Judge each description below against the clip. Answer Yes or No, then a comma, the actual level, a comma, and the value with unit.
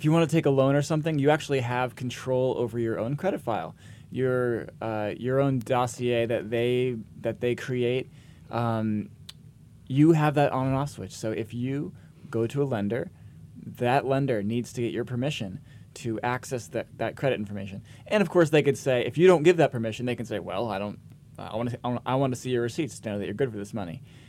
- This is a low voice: Yes, low, 125 Hz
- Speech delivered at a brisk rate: Yes, fast, 225 wpm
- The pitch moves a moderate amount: Yes, average, 3.5 semitones